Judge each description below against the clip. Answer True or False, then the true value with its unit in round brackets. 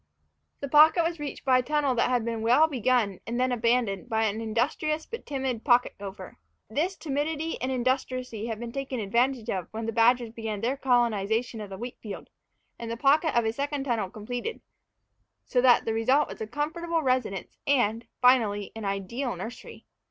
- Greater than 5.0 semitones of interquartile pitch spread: False (3.6 semitones)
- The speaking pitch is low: False (245 Hz)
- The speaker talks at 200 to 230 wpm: False (185 wpm)